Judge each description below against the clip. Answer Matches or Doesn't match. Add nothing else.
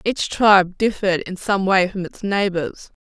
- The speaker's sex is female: Matches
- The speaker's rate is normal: Matches